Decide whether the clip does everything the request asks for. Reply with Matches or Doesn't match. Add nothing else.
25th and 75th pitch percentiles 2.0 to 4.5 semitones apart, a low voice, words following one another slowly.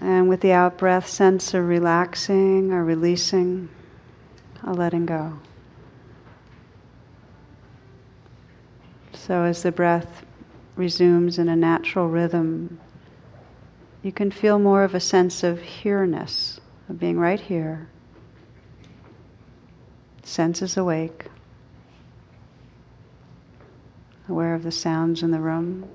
Doesn't match